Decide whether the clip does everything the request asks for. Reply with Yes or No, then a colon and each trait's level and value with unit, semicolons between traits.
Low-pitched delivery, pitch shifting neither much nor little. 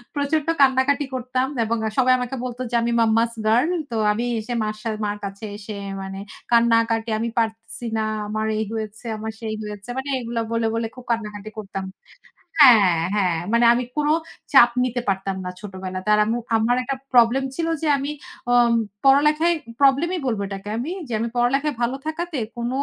No: high, 235 Hz; average, 3.3 semitones